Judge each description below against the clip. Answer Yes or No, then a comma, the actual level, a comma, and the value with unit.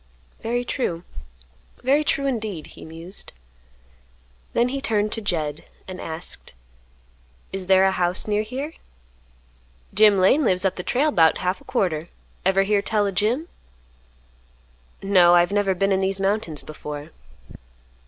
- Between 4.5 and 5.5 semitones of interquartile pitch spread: No, average, 3.8 semitones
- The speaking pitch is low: No, high, 195 Hz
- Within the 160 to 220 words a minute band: No, average, 145 wpm